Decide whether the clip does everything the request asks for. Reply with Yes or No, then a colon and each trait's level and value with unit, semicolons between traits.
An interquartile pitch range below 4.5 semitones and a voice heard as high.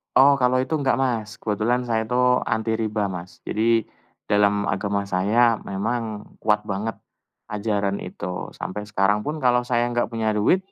No: average, 2.8 semitones; low, 110 Hz